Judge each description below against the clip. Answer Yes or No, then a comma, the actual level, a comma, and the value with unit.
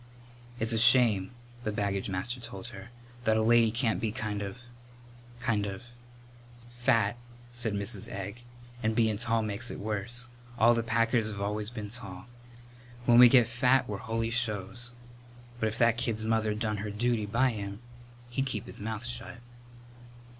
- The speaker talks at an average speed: Yes, average, 170 wpm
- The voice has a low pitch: Yes, low, 110 Hz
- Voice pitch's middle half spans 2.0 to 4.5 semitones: Yes, narrow, 2.4 semitones